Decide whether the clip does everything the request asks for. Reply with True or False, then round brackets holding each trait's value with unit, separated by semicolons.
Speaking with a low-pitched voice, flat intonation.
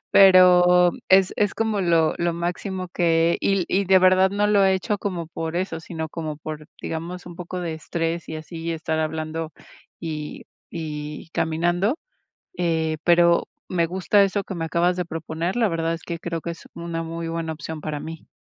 False (170 Hz; 2.1 semitones)